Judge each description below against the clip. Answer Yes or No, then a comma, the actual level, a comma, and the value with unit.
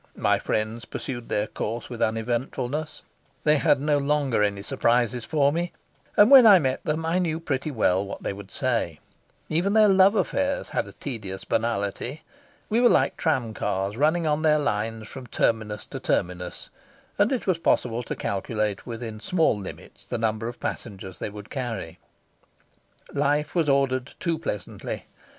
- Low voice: Yes, low, 125 Hz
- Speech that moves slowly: No, average, 165 wpm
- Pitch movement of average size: No, wide, 6.3 semitones